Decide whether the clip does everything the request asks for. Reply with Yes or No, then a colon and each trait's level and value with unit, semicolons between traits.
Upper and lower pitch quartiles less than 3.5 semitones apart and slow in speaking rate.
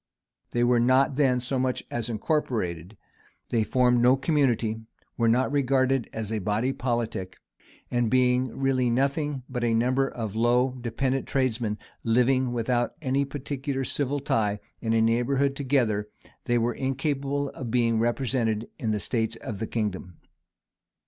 No: average, 2.8 semitones; average, 150 wpm